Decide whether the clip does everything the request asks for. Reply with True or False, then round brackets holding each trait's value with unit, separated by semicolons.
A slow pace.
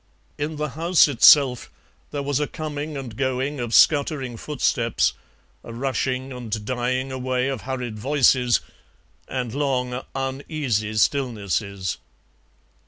True (115 wpm)